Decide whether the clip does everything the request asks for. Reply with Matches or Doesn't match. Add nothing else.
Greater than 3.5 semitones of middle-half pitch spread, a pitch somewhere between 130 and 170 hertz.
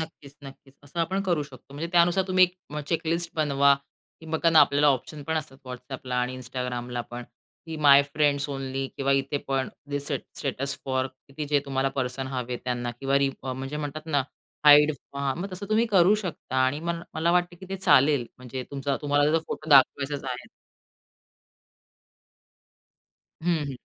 Doesn't match